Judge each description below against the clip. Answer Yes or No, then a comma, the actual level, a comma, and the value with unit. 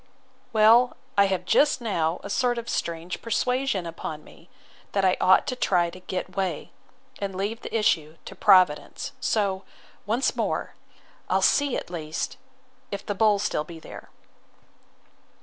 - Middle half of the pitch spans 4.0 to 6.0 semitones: Yes, average, 4.7 semitones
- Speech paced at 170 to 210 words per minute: No, average, 150 wpm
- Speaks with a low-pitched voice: No, high, 195 Hz